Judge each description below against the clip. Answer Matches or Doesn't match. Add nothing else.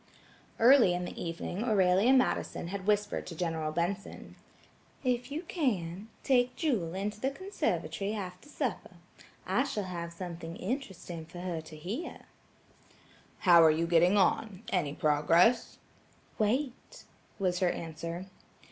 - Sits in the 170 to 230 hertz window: Matches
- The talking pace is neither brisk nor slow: Doesn't match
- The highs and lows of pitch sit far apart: Matches